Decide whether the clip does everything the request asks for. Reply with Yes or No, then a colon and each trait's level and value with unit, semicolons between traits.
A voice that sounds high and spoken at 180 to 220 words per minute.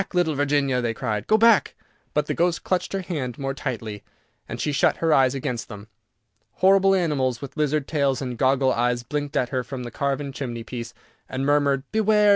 No: medium, 140 Hz; average, 190 wpm